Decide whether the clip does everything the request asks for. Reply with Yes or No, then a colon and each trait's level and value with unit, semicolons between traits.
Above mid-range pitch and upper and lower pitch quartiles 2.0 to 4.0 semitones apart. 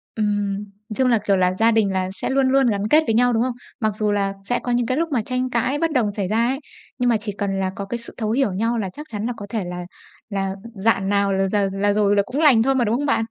Yes: high, 220 Hz; average, 3.7 semitones